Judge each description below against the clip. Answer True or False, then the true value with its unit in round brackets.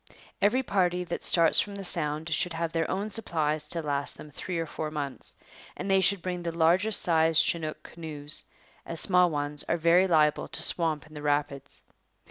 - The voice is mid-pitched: True (165 Hz)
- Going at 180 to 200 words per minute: True (190 wpm)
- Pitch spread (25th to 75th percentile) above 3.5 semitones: False (3.0 semitones)